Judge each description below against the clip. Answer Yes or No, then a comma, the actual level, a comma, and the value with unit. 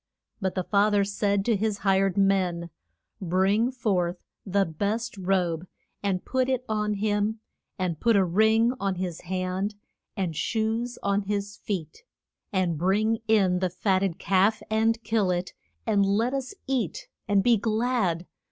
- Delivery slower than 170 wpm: Yes, average, 155 wpm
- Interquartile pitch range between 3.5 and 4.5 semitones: No, average, 2.9 semitones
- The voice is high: Yes, high, 200 Hz